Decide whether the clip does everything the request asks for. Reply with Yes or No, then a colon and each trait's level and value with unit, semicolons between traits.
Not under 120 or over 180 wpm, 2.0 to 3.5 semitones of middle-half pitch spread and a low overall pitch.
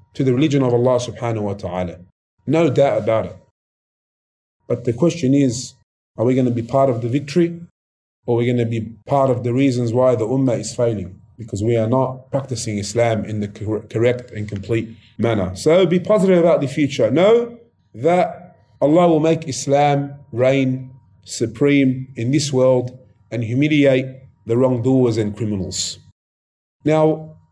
No: average, 165 wpm; average, 4.1 semitones; low, 125 Hz